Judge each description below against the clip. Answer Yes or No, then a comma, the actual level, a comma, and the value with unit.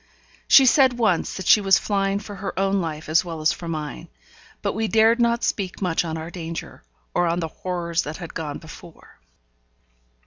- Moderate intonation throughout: Yes, average, 3.9 semitones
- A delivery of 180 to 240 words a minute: Yes, average, 195 wpm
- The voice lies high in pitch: No, medium, 180 Hz